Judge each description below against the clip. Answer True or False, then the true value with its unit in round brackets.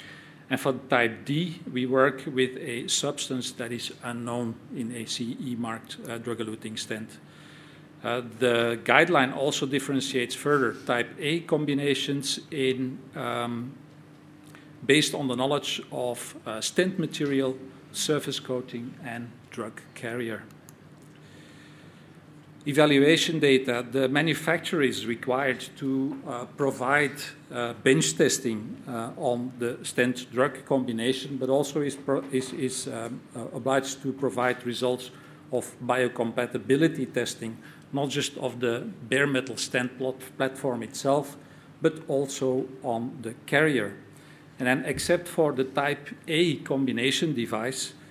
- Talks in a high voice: False (135 Hz)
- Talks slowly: True (125 wpm)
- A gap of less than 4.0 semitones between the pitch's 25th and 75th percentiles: True (2.9 semitones)